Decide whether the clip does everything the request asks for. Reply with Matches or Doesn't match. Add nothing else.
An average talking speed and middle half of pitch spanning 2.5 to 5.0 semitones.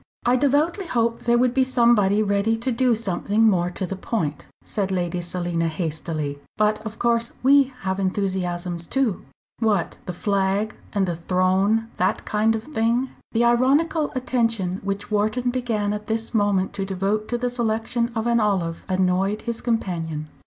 Matches